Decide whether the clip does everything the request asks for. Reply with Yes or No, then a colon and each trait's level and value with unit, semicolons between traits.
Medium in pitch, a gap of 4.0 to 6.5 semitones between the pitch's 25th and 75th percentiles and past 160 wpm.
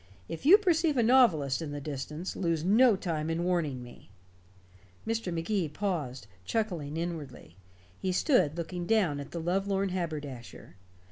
No: medium, 170 Hz; average, 5.2 semitones; average, 145 wpm